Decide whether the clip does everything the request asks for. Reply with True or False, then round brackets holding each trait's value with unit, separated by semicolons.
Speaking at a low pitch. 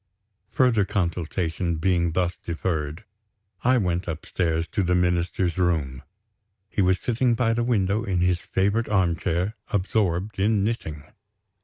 True (90 Hz)